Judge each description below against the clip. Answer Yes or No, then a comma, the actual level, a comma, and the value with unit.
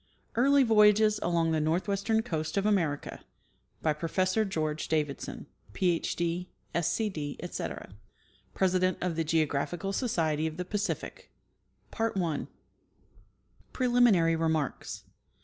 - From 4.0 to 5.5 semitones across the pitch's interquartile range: Yes, average, 4.6 semitones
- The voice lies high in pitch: No, medium, 175 Hz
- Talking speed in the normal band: No, slow, 105 wpm